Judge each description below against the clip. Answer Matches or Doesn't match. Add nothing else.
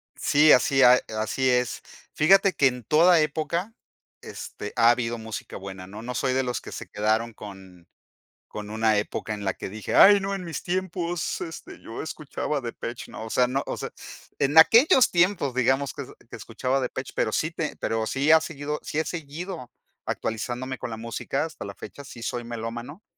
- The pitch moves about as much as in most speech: Doesn't match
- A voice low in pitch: Matches